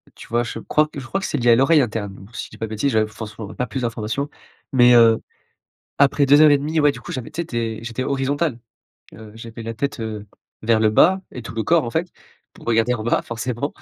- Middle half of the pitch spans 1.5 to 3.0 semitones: No, average, 4.1 semitones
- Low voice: Yes, low, 120 Hz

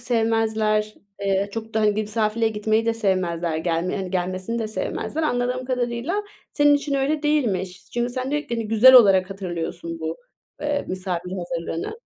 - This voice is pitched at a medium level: No, high, 215 Hz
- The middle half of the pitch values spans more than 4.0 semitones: Yes, average, 4.9 semitones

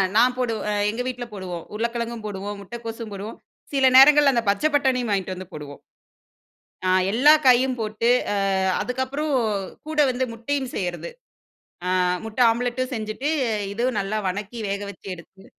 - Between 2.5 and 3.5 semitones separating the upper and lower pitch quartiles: No, average, 4.0 semitones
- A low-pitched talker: No, high, 230 Hz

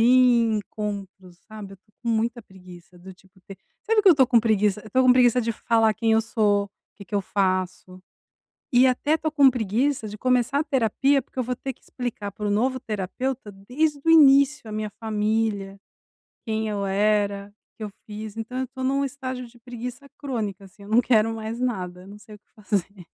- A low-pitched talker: No, high, 220 Hz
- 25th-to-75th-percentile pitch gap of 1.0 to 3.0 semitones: No, average, 3.8 semitones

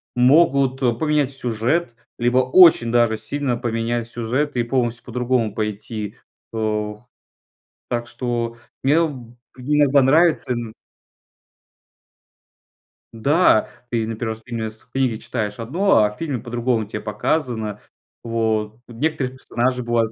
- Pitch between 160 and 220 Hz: No, low, 120 Hz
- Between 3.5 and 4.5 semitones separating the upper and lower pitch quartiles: No, average, 3.0 semitones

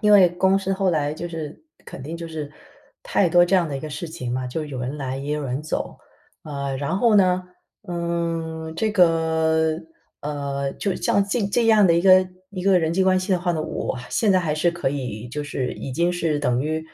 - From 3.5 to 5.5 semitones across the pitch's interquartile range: Yes, average, 4.0 semitones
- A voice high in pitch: No, medium, 165 Hz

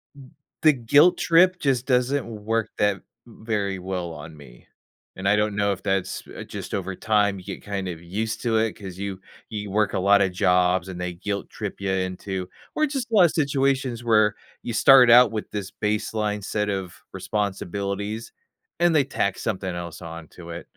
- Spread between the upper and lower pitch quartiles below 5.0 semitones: Yes, average, 3.8 semitones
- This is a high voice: No, low, 105 Hz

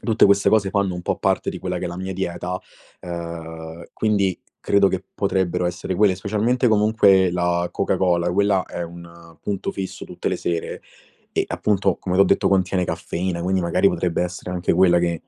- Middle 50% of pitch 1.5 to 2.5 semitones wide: Yes, narrow, 2.2 semitones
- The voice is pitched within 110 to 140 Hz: No, very low, 90 Hz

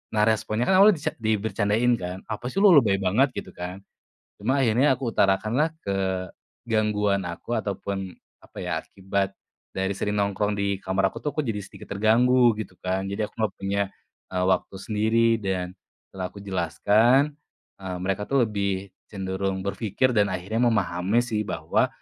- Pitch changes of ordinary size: Yes, average, 3.0 semitones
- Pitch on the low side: Yes, low, 105 Hz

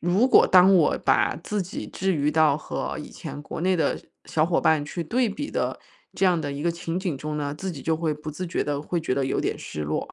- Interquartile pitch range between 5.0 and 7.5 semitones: No, average, 3.8 semitones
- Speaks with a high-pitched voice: No, medium, 160 Hz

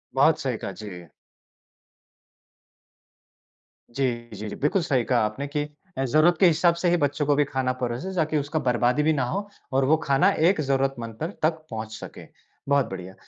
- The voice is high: No, low, 135 Hz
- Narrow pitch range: No, average, 4.5 semitones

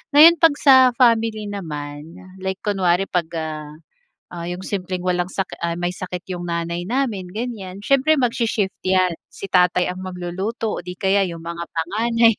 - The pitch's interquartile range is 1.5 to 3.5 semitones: No, average, 4.1 semitones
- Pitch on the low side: No, medium, 185 Hz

